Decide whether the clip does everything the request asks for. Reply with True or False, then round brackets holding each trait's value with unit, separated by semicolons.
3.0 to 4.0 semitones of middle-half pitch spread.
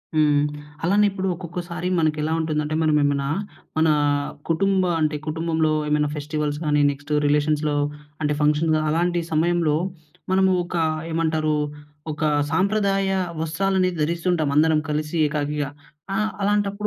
False (2.6 semitones)